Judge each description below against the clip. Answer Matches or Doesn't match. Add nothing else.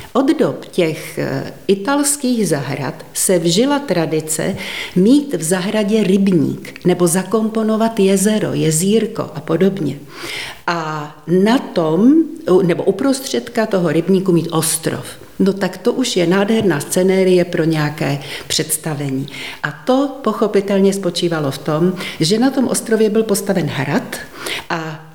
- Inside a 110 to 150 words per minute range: Matches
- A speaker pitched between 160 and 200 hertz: Matches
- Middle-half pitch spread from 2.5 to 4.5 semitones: Doesn't match